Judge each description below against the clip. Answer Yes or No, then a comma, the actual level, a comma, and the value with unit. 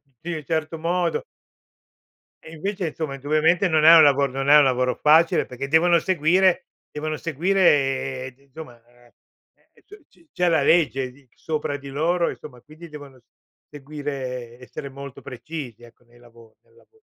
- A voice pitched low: No, medium, 145 Hz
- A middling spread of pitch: Yes, average, 3.8 semitones